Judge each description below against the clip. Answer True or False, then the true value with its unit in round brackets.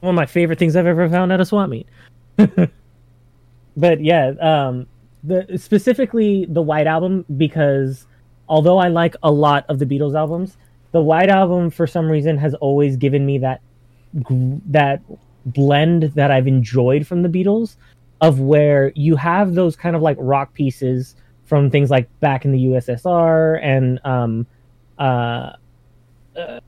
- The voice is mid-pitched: True (145 Hz)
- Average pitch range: True (4.9 semitones)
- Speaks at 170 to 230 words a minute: False (155 wpm)